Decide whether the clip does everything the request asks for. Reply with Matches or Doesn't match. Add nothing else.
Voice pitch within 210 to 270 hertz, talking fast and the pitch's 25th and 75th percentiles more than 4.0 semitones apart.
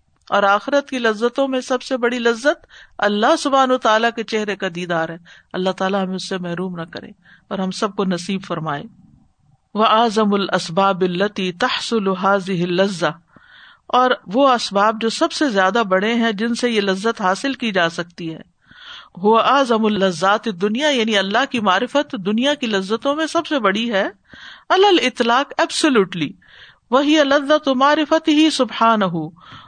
Doesn't match